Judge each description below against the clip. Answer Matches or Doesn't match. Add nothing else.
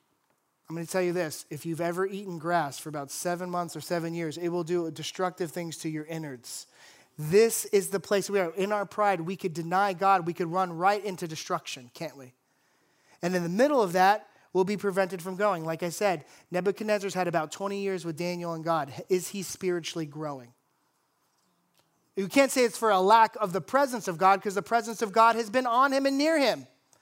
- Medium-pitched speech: Matches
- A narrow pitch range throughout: Doesn't match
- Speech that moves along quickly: Matches